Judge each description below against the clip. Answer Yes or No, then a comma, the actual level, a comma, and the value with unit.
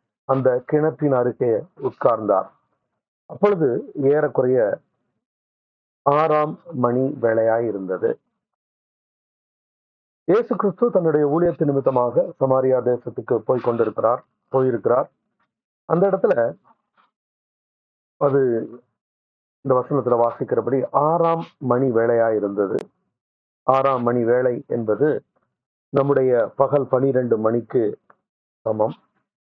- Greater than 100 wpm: No, average, 80 wpm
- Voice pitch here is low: Yes, low, 130 Hz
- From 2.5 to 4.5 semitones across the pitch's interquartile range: Yes, average, 4.1 semitones